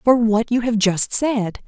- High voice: Yes, high, 225 Hz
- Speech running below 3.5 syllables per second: No, 3.9 syllables/s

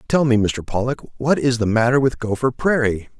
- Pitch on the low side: Yes, low, 120 Hz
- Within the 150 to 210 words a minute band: Yes, fast, 205 wpm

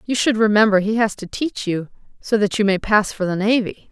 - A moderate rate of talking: No, fast, 245 wpm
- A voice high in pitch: Yes, high, 210 Hz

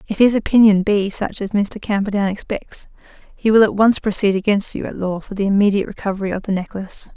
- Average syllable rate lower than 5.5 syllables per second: No, 6.0 syllables/s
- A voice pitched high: Yes, high, 200 Hz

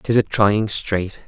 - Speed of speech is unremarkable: Yes, average, 190 wpm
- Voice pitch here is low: Yes, low, 105 Hz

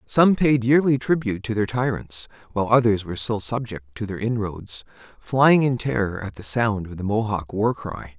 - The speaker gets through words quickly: No, average, 190 wpm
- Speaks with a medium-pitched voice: No, low, 110 Hz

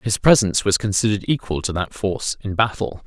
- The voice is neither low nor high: No, low, 105 Hz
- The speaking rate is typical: Yes, average, 195 wpm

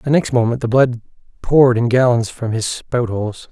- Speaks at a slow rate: No, fast, 205 wpm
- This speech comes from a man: Yes, male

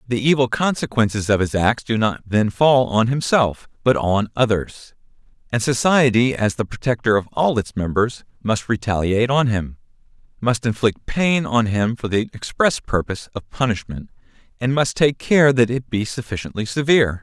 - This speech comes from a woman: No, male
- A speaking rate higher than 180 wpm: No, average, 165 wpm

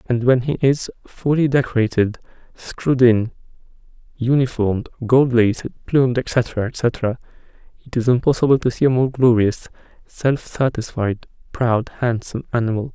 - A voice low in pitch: Yes, low, 120 Hz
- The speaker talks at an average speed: No, slow, 120 wpm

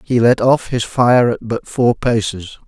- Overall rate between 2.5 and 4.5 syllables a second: Yes, 4.1 syllables/s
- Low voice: Yes, low, 115 Hz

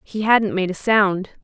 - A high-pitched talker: Yes, high, 200 Hz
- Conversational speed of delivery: No, fast, 210 wpm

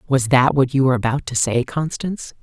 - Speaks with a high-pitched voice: No, low, 130 Hz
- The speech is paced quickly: Yes, fast, 225 wpm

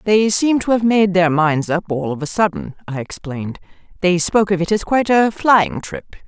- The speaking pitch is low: No, medium, 185 Hz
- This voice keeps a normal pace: No, fast, 220 wpm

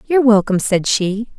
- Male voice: No, female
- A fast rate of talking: No, average, 175 wpm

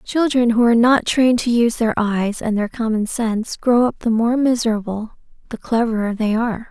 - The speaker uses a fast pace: No, average, 195 wpm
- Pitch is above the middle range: Yes, high, 230 Hz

